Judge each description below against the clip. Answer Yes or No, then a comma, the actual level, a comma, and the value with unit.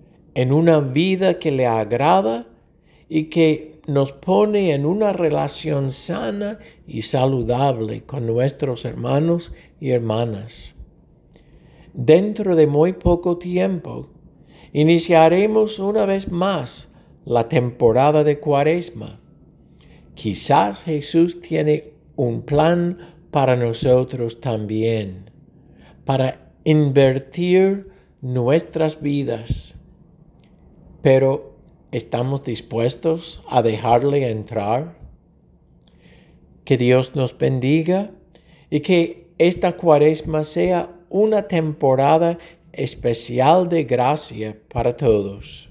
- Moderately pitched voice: Yes, medium, 150 Hz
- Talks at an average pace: No, slow, 90 wpm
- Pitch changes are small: No, average, 5.3 semitones